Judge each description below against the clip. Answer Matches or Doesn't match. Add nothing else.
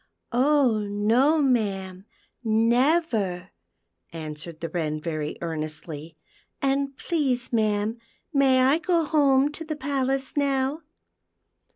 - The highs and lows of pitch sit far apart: Matches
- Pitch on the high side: Matches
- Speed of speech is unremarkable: Doesn't match